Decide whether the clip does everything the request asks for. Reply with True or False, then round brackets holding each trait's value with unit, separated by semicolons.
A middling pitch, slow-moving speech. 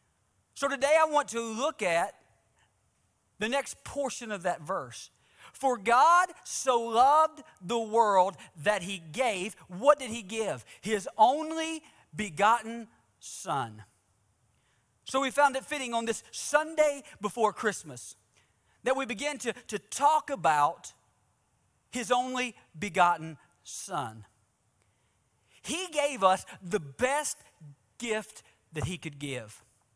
False (220 Hz; 120 wpm)